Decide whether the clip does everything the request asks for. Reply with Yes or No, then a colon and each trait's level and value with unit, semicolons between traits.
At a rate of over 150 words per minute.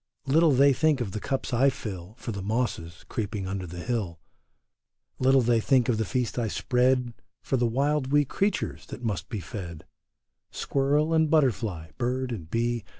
Yes: average, 175 wpm